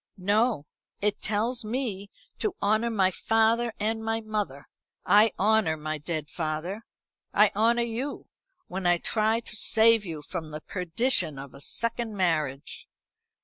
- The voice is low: No, high, 210 Hz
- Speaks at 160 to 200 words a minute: No, average, 145 wpm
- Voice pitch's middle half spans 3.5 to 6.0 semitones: Yes, average, 5.2 semitones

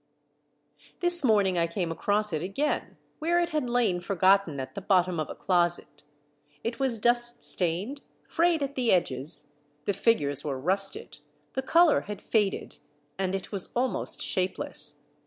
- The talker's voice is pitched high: Yes, high, 200 Hz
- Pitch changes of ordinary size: No, wide, 5.9 semitones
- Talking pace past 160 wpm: No, average, 155 wpm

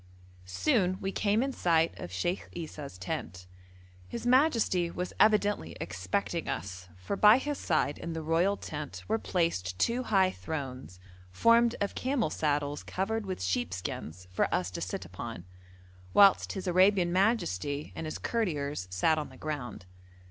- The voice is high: No, medium, 165 Hz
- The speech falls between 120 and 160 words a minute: Yes, average, 150 wpm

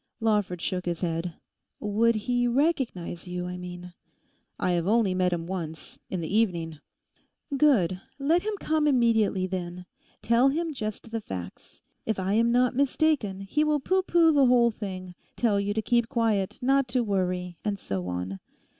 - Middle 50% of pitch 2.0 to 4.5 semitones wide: No, wide, 5.6 semitones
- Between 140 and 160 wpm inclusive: No, average, 170 wpm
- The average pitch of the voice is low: No, high, 210 Hz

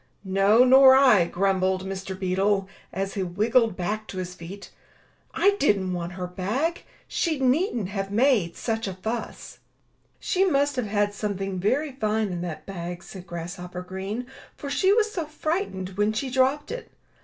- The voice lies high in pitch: Yes, high, 205 Hz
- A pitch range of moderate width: No, wide, 5.8 semitones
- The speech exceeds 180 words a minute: No, average, 165 wpm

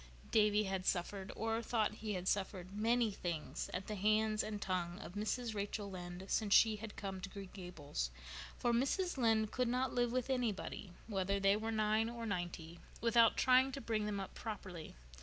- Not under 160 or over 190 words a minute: Yes, average, 185 wpm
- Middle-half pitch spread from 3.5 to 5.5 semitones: No, average, 3.0 semitones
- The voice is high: Yes, high, 210 Hz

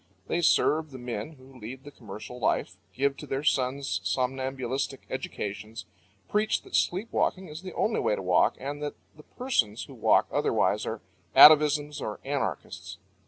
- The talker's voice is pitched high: No, low, 135 Hz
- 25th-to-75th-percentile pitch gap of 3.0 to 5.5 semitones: Yes, average, 3.8 semitones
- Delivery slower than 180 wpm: Yes, average, 165 wpm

